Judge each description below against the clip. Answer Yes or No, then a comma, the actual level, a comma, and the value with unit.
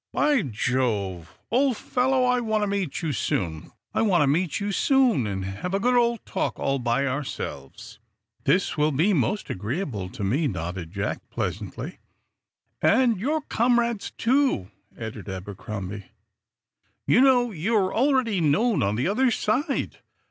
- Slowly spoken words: Yes, slow, 130 wpm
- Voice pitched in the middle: Yes, medium, 180 Hz